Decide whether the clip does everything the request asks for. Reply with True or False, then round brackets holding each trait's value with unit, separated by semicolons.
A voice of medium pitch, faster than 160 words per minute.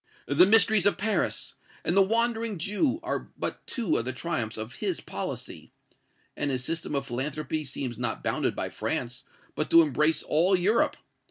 True (165 Hz; 170 wpm)